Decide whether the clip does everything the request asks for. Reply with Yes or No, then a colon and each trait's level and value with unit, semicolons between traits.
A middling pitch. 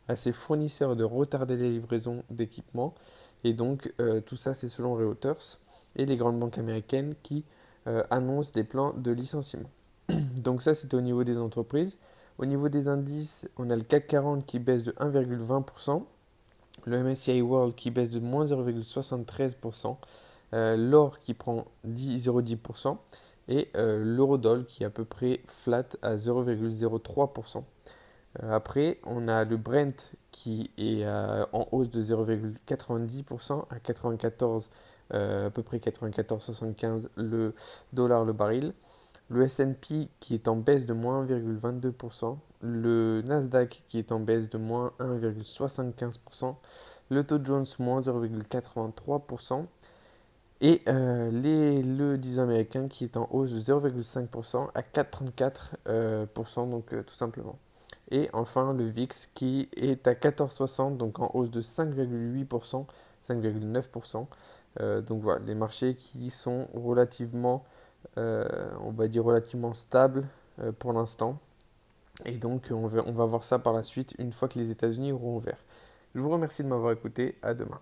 No: low, 120 Hz